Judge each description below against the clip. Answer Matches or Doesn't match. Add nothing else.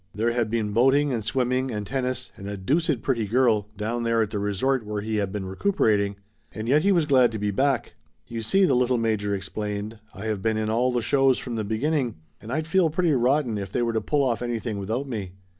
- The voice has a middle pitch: Doesn't match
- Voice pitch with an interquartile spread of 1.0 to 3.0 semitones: Doesn't match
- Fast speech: Matches